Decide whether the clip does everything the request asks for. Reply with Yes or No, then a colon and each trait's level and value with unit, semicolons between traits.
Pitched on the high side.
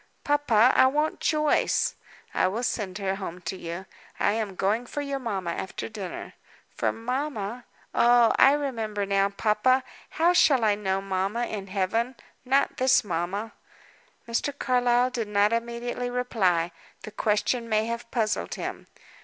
Yes: high, 225 Hz